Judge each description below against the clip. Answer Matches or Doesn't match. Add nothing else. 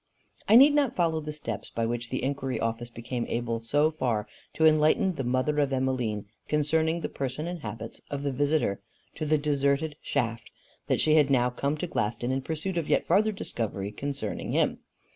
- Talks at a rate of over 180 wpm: Matches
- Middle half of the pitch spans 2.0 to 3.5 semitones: Doesn't match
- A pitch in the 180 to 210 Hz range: Doesn't match